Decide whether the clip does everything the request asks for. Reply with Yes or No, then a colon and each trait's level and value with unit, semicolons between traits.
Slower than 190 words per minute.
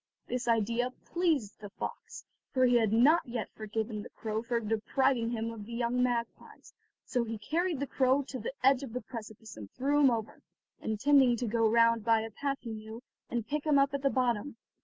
No: fast, 205 wpm